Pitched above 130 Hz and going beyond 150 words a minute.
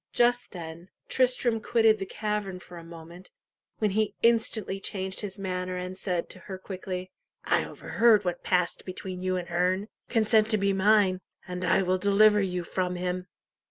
Yes: high, 190 Hz; average, 170 wpm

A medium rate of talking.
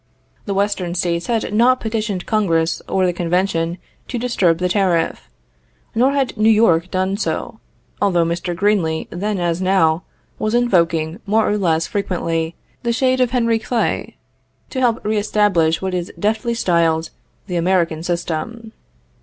Yes: average, 150 wpm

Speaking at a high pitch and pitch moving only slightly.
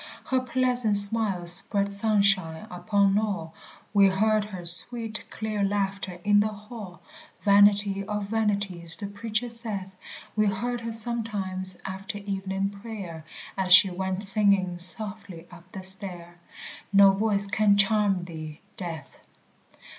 Yes: high, 200 Hz; narrow, 2.3 semitones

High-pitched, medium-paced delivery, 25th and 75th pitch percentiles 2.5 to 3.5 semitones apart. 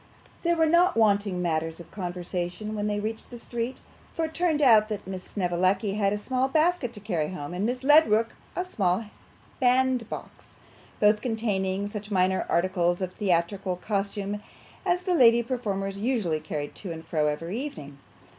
No: high, 205 Hz; average, 165 wpm; average, 4.9 semitones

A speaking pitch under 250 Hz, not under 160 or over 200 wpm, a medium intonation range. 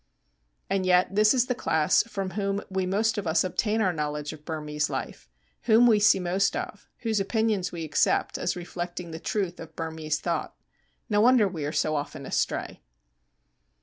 Yes: medium, 185 Hz; average, 180 wpm; average, 4.7 semitones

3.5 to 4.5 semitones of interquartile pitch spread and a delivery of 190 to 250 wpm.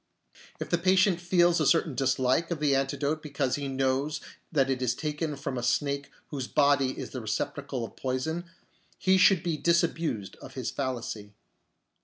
No: average, 4.0 semitones; average, 170 wpm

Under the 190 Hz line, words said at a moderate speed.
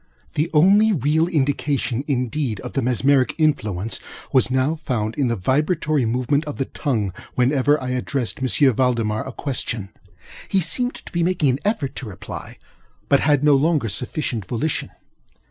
Yes: low, 135 Hz; average, 160 wpm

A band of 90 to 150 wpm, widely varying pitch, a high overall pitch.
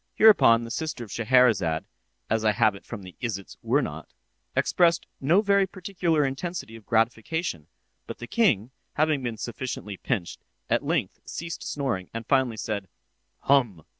No: average, 145 wpm; wide, 6.6 semitones; low, 120 Hz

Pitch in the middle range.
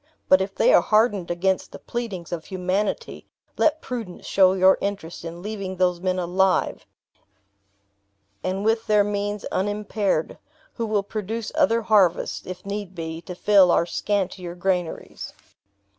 No: high, 195 Hz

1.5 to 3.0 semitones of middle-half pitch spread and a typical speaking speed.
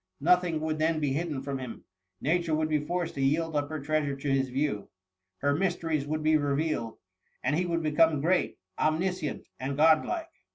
Yes: average, 2.7 semitones; average, 195 wpm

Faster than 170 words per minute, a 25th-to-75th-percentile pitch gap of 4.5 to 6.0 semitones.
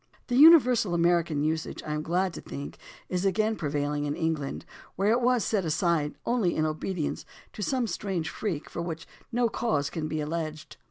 Yes: average, 180 wpm; wide, 5.4 semitones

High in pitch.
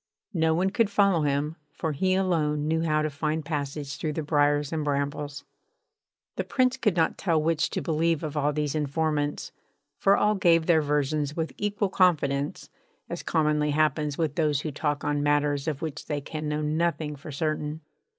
No: medium, 155 Hz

